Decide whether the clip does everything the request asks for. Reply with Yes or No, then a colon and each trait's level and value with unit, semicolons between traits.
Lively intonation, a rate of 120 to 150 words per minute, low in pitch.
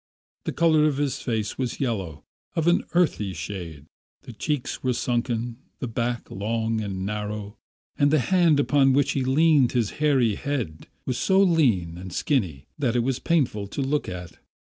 No: wide, 5.7 semitones; average, 170 wpm; low, 120 Hz